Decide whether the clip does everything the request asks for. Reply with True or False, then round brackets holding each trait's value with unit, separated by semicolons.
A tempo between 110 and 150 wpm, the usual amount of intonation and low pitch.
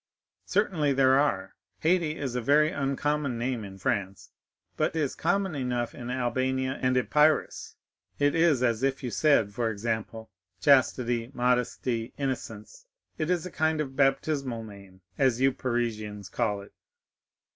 True (140 wpm; 4.2 semitones; 130 Hz)